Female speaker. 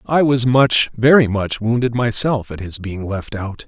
No: male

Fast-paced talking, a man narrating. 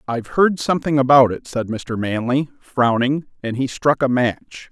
No: average, 180 wpm; male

